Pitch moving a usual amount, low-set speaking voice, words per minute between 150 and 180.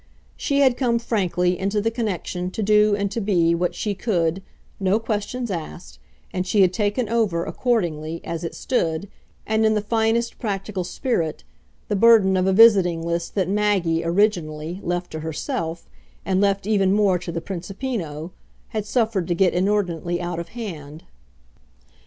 No: average, 3.9 semitones; high, 190 Hz; average, 165 wpm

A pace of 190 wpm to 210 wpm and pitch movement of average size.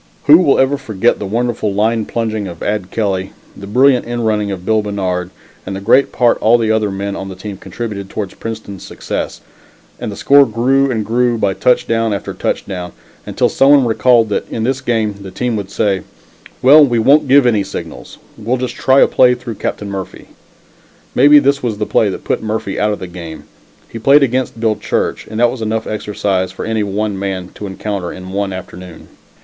Yes: fast, 205 wpm; average, 3.6 semitones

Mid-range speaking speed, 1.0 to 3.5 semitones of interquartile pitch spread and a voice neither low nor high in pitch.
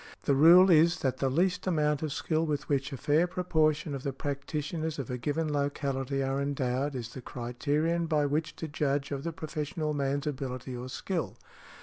Yes: average, 190 wpm; narrow, 2.6 semitones; medium, 145 Hz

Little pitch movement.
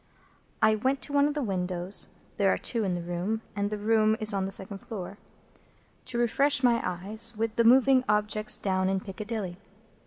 No: average, 3.3 semitones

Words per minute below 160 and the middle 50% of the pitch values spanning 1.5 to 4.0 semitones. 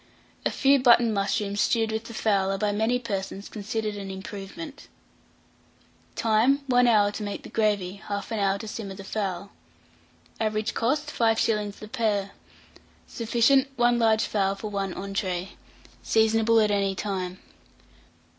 Yes: average, 145 wpm; narrow, 2.4 semitones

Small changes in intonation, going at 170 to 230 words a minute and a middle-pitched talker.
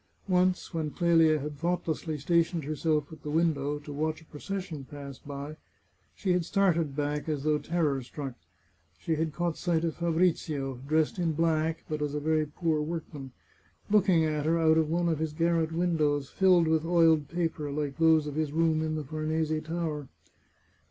Yes: narrow, 2.0 semitones; average, 180 wpm; medium, 160 Hz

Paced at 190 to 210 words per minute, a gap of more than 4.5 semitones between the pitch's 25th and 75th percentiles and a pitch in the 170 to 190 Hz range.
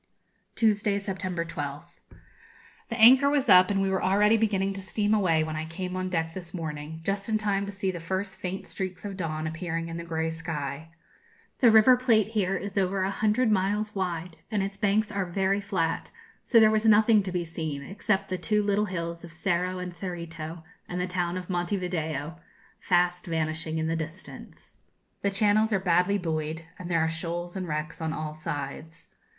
No: average, 195 wpm; average, 3.4 semitones; medium, 185 Hz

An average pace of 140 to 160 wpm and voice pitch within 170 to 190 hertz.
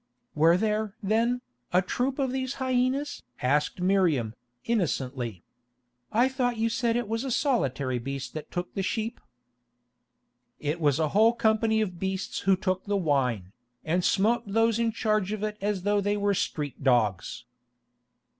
No: average, 155 wpm; high, 200 Hz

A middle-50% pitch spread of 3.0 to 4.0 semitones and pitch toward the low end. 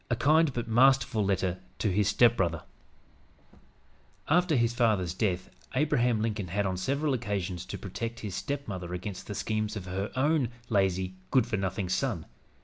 No: average, 4.6 semitones; low, 105 Hz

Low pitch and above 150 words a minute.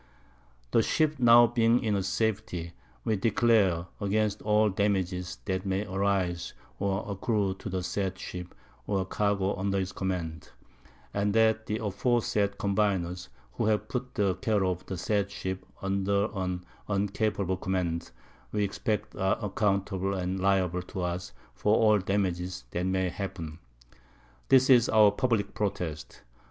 No: low, 100 Hz; average, 140 wpm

